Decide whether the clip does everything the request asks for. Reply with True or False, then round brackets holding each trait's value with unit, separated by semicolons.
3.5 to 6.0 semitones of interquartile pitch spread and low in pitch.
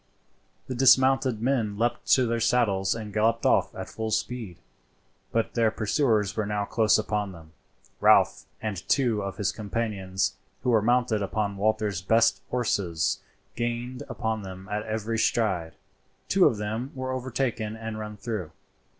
False (2.5 semitones; 110 Hz)